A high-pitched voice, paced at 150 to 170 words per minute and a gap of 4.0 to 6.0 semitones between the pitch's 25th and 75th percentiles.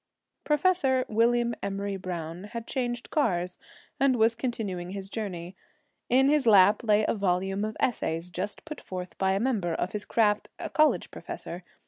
Yes: high, 210 Hz; average, 160 wpm; average, 4.6 semitones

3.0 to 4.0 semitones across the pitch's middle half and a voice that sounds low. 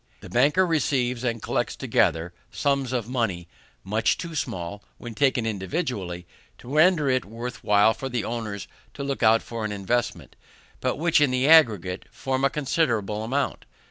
No: average, 4.6 semitones; low, 120 Hz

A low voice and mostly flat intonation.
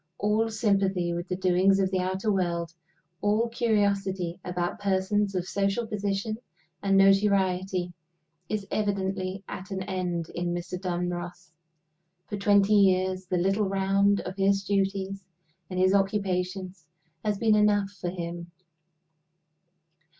No: high, 195 Hz; narrow, 1.8 semitones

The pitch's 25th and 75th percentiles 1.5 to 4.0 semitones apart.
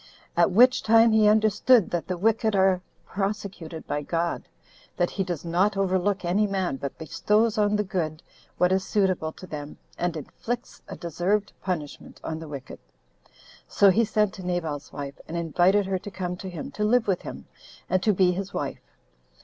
Yes: average, 3.6 semitones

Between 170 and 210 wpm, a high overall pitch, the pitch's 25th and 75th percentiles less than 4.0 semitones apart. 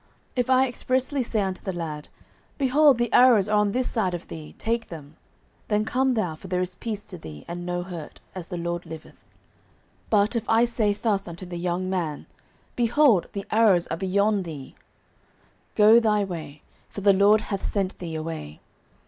No: average, 190 wpm; high, 195 Hz; average, 4.6 semitones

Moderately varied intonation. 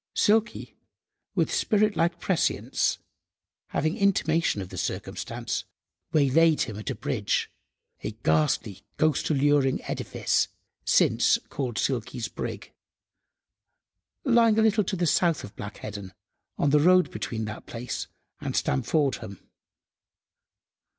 No: wide, 8.3 semitones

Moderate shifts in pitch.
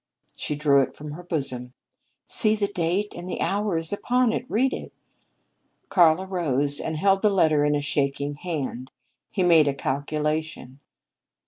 Yes: average, 4.9 semitones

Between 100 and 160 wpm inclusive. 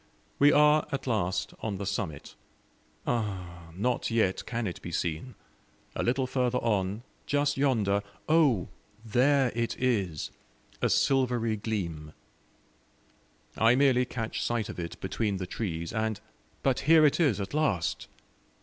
Yes: average, 140 wpm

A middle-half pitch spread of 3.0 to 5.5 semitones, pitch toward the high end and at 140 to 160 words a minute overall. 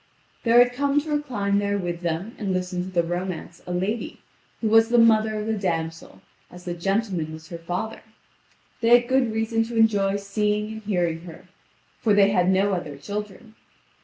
No: average, 4.0 semitones; high, 200 Hz; average, 190 wpm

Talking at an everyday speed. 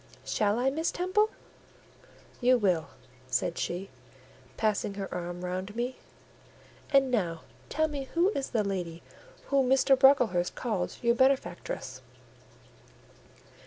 No: slow, 120 wpm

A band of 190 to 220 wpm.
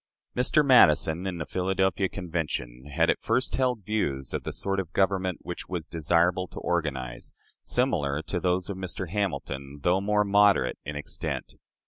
No: average, 165 wpm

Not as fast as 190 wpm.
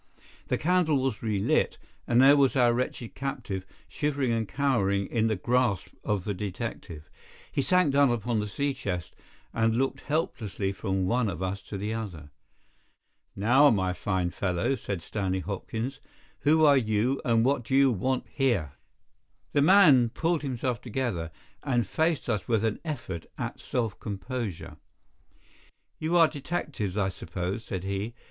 Yes: average, 155 wpm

